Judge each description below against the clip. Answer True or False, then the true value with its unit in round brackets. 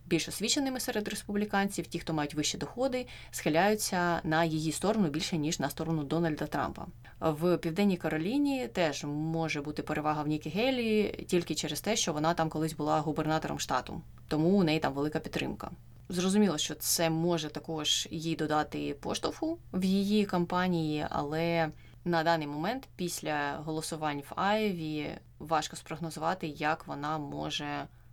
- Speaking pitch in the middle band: True (160 Hz)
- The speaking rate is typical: True (145 wpm)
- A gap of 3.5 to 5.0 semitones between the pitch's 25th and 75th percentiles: False (3.0 semitones)